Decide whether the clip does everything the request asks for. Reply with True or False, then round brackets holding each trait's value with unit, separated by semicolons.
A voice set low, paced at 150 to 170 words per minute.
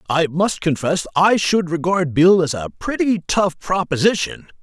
False (170 Hz; 155 wpm)